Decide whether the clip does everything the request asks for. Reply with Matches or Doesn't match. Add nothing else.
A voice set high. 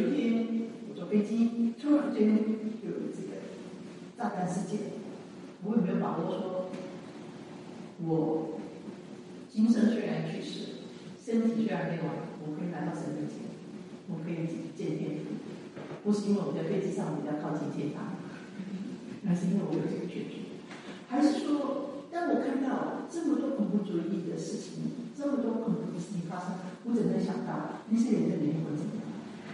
Matches